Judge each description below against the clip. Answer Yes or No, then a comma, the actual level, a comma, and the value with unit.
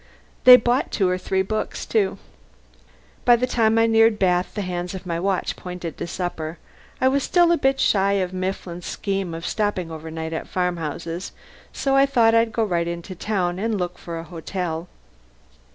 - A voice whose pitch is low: No, medium, 185 Hz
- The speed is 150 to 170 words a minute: No, average, 185 wpm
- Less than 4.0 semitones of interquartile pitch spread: No, average, 4.4 semitones